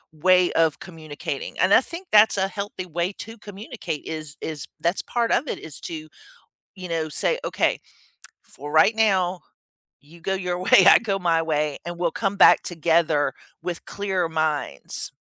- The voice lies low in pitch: No, medium, 175 Hz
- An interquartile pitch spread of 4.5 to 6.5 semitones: No, average, 3.6 semitones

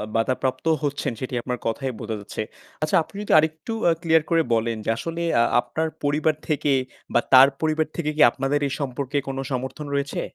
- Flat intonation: No, average, 3.5 semitones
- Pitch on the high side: No, medium, 140 Hz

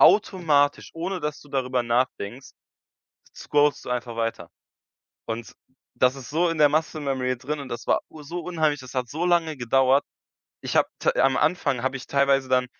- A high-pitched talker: No, medium, 140 Hz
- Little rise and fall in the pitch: No, average, 3.2 semitones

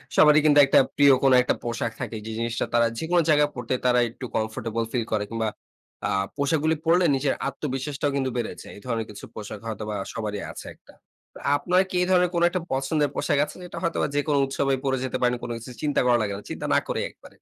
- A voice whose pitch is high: No, low, 135 Hz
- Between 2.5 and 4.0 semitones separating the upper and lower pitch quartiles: No, average, 4.4 semitones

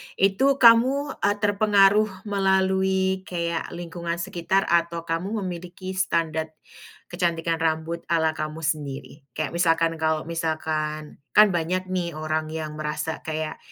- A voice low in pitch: No, medium, 170 Hz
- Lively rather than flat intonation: No, average, 3.0 semitones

